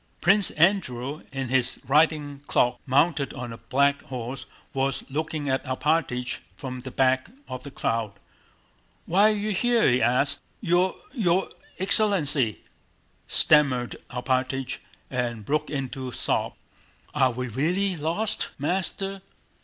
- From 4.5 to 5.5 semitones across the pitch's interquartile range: Yes, average, 5.2 semitones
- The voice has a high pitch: No, medium, 140 Hz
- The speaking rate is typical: No, slow, 125 wpm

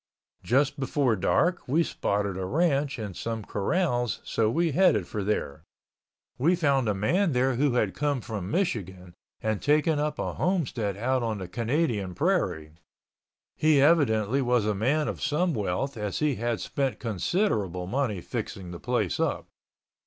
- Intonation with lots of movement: Yes, wide, 6.3 semitones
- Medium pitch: No, low, 120 Hz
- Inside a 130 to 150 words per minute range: No, average, 160 wpm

